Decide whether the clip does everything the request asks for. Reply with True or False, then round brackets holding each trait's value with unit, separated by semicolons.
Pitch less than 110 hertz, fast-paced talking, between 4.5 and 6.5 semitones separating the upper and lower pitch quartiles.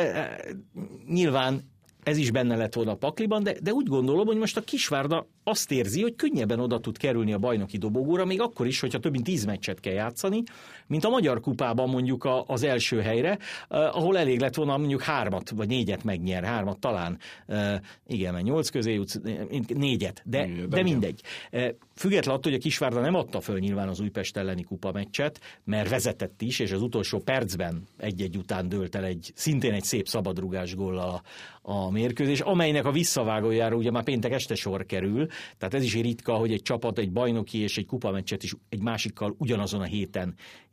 False (115 Hz; 185 wpm; 5.5 semitones)